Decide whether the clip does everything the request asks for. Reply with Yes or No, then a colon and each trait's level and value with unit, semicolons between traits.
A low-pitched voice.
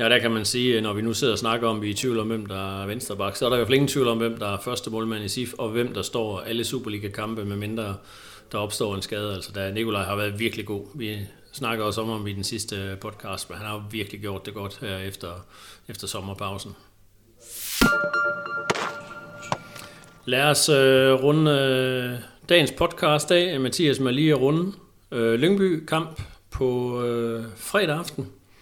Yes: low, 115 Hz